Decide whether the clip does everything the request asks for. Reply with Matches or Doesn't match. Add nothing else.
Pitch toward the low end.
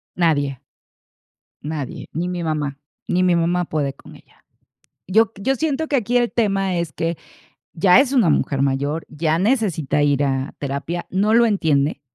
Doesn't match